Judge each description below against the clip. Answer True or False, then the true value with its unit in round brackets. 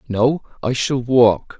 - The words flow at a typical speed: True (150 wpm)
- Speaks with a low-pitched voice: True (125 Hz)